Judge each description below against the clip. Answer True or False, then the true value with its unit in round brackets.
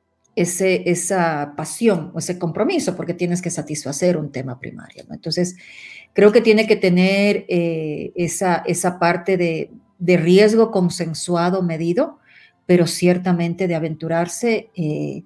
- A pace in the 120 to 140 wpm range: True (135 wpm)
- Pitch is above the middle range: False (175 Hz)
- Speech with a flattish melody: True (2.3 semitones)